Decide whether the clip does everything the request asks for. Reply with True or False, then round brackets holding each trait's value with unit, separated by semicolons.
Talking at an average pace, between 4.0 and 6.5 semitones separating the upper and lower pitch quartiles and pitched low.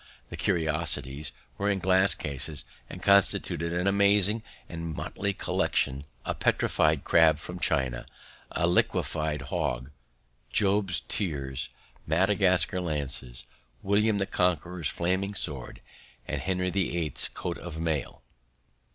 False (115 wpm; 4.3 semitones; 85 Hz)